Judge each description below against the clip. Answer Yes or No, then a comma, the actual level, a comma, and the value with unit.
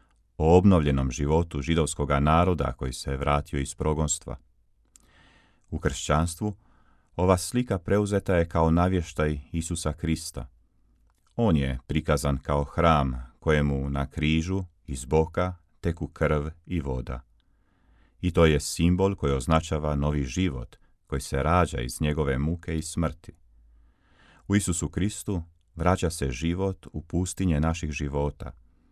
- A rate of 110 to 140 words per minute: Yes, average, 125 wpm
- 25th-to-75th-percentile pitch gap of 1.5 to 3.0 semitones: No, average, 3.5 semitones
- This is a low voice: Yes, very low, 80 Hz